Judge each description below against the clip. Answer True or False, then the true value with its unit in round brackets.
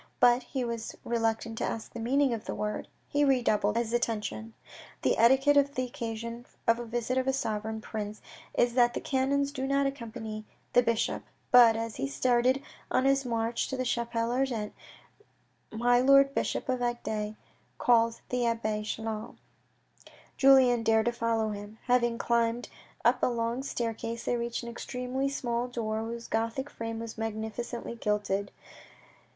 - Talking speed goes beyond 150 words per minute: True (160 wpm)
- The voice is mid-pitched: False (235 Hz)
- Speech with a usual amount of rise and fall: False (1.9 semitones)